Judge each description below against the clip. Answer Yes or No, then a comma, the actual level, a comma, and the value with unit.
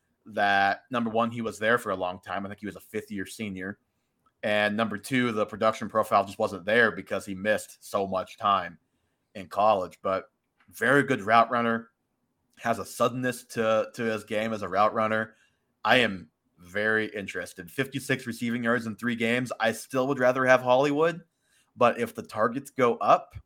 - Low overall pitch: Yes, low, 115 Hz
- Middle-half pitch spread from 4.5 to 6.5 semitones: No, average, 2.9 semitones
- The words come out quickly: No, average, 185 wpm